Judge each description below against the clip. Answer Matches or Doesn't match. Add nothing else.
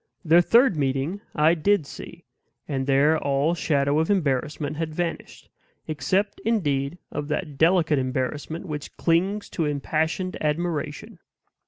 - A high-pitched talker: Doesn't match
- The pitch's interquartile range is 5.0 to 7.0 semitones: Doesn't match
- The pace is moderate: Doesn't match